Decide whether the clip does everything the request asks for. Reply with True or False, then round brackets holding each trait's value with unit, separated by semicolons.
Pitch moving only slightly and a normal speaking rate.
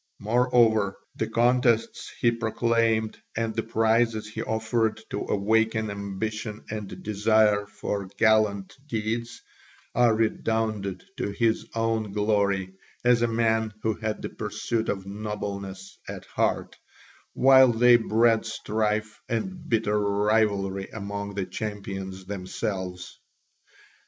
False (1.9 semitones; 115 wpm)